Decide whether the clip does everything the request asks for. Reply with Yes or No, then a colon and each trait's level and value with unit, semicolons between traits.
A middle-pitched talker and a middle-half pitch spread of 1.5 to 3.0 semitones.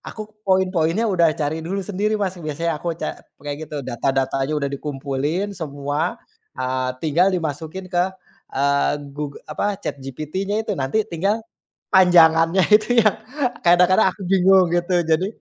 No: medium, 170 Hz; average, 4.5 semitones